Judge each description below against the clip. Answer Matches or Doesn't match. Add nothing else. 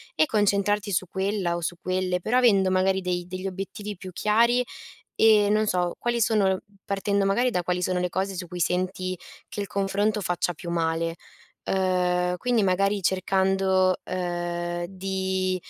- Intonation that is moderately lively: Doesn't match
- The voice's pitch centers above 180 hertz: Matches